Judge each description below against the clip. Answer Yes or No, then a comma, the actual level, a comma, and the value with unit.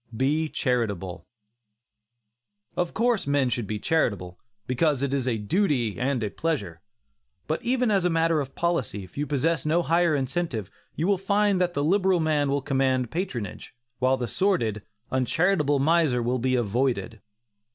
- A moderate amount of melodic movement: No, wide, 5.7 semitones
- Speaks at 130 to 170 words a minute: Yes, average, 160 wpm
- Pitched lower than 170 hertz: Yes, medium, 140 Hz